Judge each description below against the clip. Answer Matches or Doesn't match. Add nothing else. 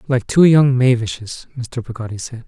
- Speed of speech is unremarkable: Matches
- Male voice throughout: Matches